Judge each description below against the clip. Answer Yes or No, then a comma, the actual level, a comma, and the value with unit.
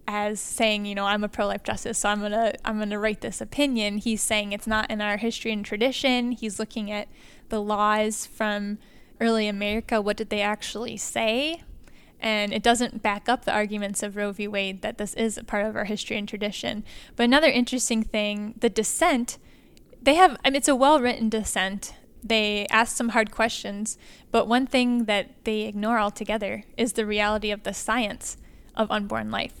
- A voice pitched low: No, high, 220 Hz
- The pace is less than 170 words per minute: No, average, 195 wpm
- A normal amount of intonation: No, narrow, 2.2 semitones